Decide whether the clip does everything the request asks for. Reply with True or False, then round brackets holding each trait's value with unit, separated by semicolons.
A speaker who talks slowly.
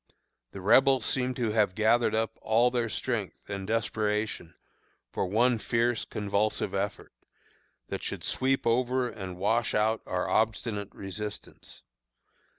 True (130 wpm)